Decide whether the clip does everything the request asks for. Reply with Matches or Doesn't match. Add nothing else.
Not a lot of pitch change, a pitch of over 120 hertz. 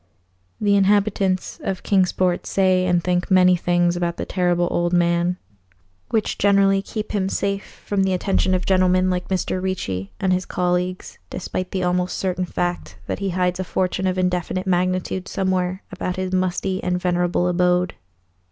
Matches